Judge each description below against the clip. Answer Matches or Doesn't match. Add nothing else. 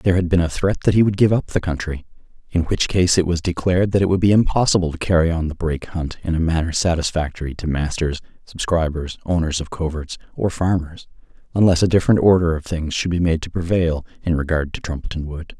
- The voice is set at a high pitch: Doesn't match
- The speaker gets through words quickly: Matches